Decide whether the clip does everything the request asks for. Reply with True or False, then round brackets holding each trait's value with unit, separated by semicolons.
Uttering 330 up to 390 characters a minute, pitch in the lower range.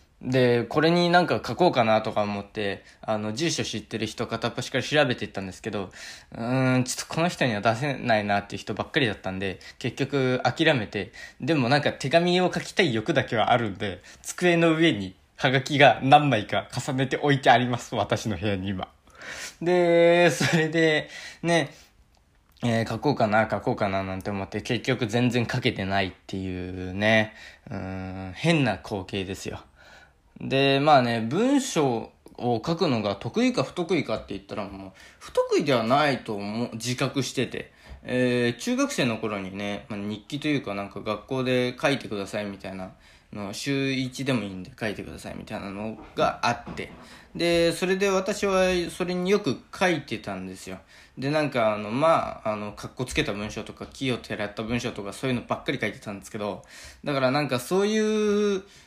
True (355 characters per minute; 125 Hz)